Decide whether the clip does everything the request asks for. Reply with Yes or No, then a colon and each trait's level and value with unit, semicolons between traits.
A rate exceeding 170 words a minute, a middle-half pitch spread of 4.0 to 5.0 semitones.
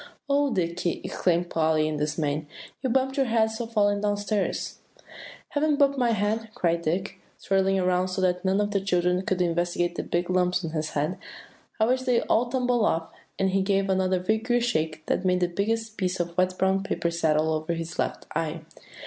Yes: average, 195 wpm; average, 4.3 semitones